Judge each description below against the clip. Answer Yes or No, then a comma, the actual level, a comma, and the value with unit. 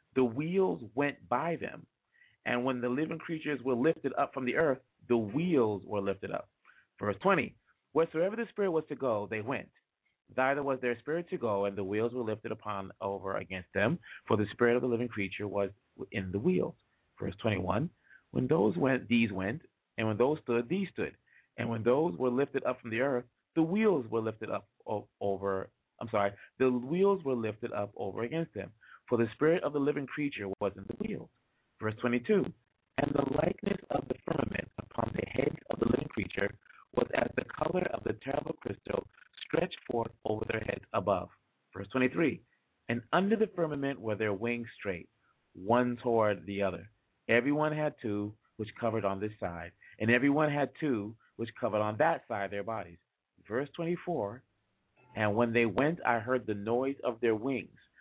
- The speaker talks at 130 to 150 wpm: No, average, 190 wpm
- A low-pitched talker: Yes, low, 120 Hz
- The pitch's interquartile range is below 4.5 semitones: No, average, 5.2 semitones